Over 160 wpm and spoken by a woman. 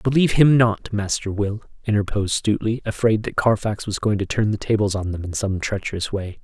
No: fast, 205 wpm; male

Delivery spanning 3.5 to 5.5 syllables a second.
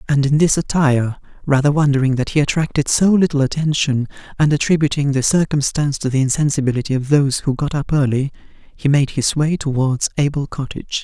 No: 6.0 syllables/s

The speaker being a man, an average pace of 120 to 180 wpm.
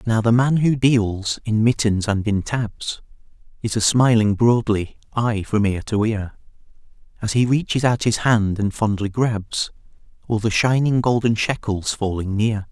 Yes: male; average, 160 wpm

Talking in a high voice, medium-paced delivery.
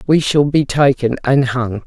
No: low, 135 Hz; average, 195 wpm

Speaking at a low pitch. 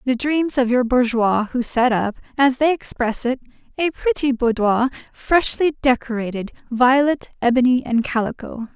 No: very high, 250 Hz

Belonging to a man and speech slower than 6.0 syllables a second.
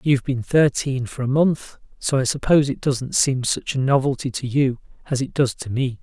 Yes: male; 5.2 syllables/s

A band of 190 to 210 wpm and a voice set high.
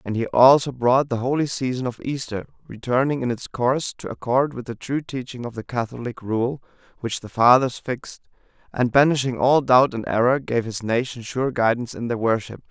No: average, 195 wpm; low, 125 Hz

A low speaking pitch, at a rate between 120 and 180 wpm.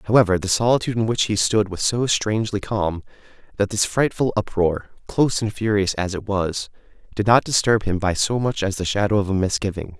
No: low, 105 Hz; fast, 205 wpm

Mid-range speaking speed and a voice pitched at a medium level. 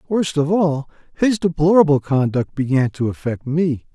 Yes: average, 150 wpm; medium, 155 Hz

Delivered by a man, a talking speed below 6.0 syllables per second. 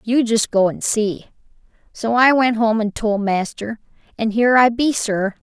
No: female; 4.5 syllables/s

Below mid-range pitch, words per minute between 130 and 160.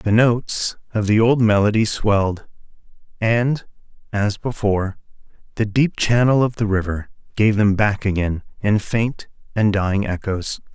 Yes: low, 105 Hz; average, 140 wpm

